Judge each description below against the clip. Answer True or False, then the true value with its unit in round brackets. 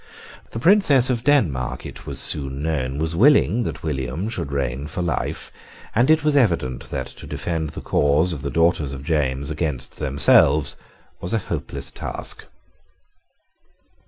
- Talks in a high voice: False (80 Hz)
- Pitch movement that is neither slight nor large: False (7.9 semitones)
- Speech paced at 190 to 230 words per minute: False (155 wpm)